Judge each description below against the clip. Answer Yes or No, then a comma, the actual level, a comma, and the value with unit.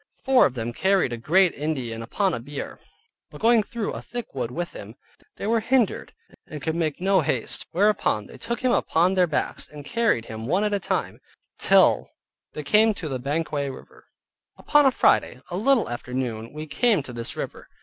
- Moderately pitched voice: Yes, medium, 160 Hz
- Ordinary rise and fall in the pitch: No, wide, 8.6 semitones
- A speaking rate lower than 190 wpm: No, average, 195 wpm